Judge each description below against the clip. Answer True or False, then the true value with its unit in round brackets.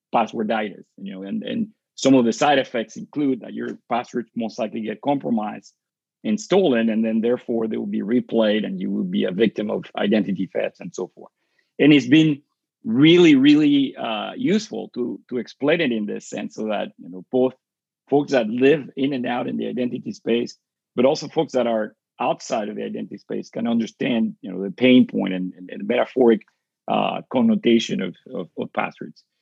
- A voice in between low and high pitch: False (130 Hz)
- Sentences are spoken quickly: False (190 wpm)